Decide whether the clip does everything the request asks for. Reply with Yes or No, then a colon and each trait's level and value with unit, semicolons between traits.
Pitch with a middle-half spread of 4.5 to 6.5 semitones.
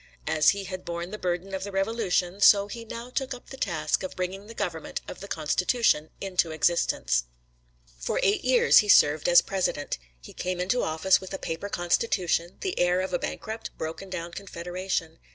No: average, 3.0 semitones